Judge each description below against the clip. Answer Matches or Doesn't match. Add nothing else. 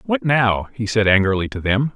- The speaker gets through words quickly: Matches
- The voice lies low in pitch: Matches